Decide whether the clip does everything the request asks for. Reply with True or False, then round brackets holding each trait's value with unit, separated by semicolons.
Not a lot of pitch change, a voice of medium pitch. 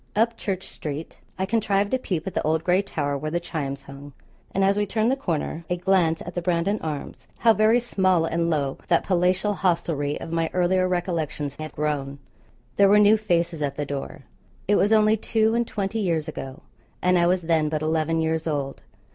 False (4.1 semitones; 170 Hz)